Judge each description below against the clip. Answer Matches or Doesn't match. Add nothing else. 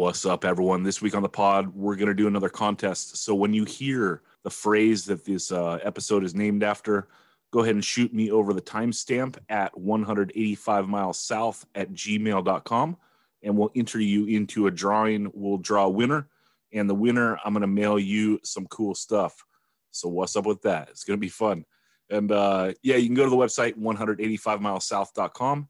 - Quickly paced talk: Doesn't match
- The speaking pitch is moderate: Doesn't match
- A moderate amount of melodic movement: Doesn't match